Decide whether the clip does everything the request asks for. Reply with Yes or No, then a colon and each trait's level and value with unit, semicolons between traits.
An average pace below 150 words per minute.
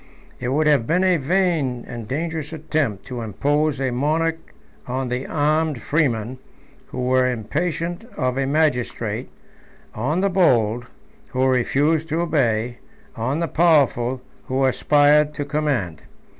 Yes: slow, 135 wpm